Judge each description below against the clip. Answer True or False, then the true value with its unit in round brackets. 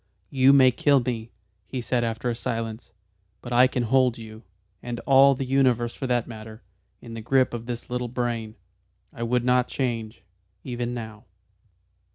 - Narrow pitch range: True (1.9 semitones)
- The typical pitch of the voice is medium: False (120 Hz)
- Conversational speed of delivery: True (170 wpm)